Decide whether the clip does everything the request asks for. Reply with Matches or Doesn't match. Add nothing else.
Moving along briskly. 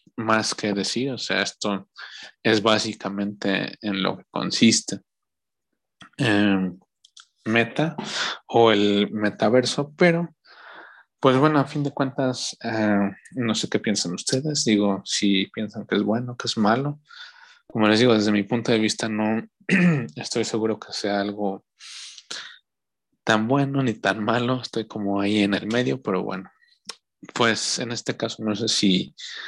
Doesn't match